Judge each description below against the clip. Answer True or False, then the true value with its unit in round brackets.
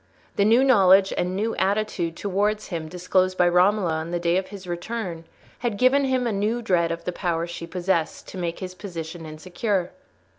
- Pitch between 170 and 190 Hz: True (185 Hz)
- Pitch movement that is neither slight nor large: True (3.3 semitones)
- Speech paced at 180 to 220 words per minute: True (190 wpm)